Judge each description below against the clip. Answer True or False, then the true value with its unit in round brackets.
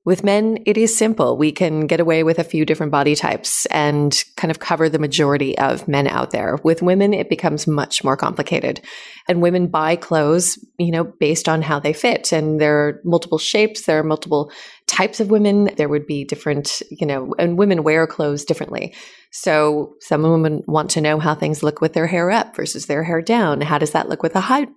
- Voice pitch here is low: False (160 Hz)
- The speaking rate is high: True (215 wpm)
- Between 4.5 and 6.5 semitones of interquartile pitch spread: False (2.8 semitones)